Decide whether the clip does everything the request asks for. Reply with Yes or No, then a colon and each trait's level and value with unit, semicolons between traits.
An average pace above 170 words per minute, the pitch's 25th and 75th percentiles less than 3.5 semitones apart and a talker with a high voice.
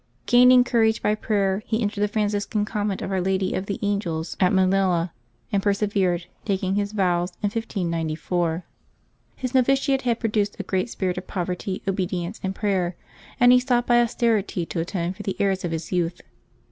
Yes: average, 180 wpm; average, 3.0 semitones; high, 195 Hz